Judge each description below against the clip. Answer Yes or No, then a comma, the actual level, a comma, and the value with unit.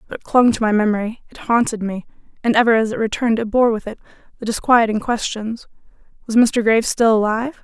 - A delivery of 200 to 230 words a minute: Yes, fast, 205 wpm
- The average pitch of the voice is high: Yes, high, 225 Hz